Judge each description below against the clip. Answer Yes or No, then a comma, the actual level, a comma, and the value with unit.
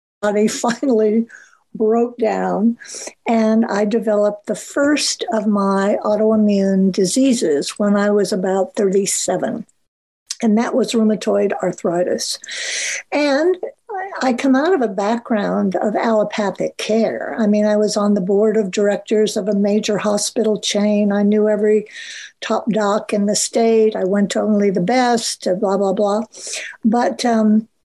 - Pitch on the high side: Yes, high, 215 Hz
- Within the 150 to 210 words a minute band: No, average, 140 wpm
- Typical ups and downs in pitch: No, narrow, 2.0 semitones